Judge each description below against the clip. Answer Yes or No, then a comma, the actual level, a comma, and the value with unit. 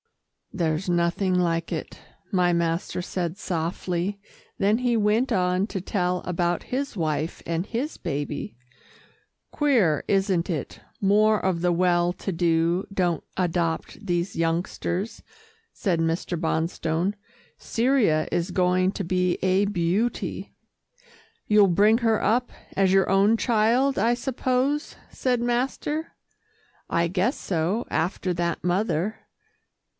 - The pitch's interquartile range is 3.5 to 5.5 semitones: Yes, average, 3.9 semitones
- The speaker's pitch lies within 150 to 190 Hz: Yes, medium, 185 Hz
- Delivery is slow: Yes, slow, 120 wpm